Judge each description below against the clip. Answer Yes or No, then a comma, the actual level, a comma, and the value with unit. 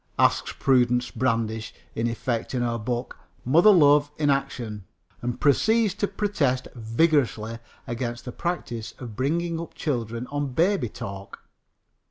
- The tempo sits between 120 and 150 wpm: Yes, slow, 135 wpm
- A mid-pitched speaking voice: No, low, 125 Hz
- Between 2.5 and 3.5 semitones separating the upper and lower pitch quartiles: No, average, 4.7 semitones